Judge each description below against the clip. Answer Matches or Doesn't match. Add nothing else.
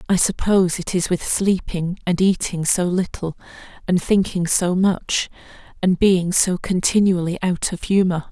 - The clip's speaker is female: Matches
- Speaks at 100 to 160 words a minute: Matches